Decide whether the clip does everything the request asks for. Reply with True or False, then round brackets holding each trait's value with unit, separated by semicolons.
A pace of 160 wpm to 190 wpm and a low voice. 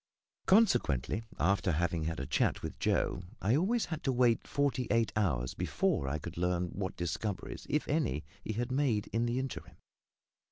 True (170 wpm; 105 Hz)